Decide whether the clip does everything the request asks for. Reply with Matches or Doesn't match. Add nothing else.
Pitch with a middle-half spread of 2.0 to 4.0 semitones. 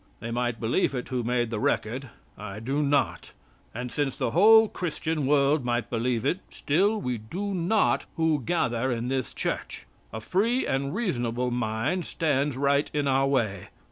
Doesn't match